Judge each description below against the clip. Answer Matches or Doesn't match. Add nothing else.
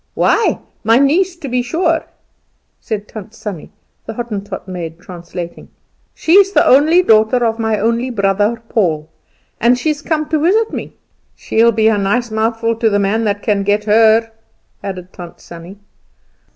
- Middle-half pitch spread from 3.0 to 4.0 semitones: Matches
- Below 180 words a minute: Matches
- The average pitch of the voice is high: Matches